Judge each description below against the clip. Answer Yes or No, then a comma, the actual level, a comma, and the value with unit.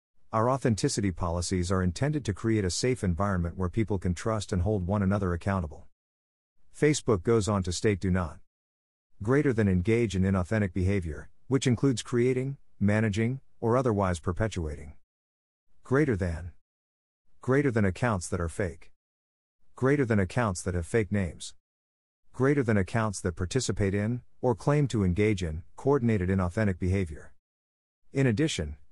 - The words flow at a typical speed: Yes, average, 145 wpm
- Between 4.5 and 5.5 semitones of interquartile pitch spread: Yes, average, 5.0 semitones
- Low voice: Yes, low, 100 Hz